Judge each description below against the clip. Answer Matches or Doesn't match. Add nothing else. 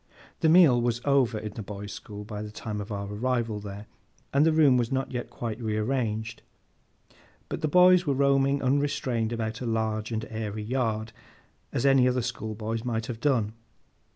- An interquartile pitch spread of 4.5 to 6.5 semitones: Doesn't match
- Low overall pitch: Matches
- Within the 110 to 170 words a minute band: Doesn't match